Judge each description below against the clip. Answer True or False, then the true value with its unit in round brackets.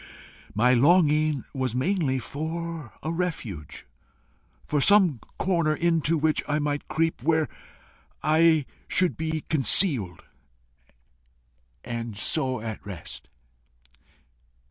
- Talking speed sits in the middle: False (100 wpm)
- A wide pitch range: False (4.4 semitones)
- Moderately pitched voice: True (150 Hz)